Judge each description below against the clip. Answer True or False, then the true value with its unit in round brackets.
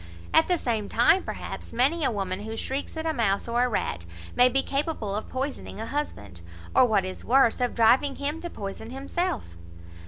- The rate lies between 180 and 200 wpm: True (195 wpm)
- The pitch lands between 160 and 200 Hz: False (245 Hz)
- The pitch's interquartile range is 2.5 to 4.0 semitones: False (5.2 semitones)